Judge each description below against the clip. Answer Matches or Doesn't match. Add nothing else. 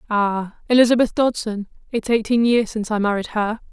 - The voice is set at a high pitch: Matches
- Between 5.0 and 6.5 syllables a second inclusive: Matches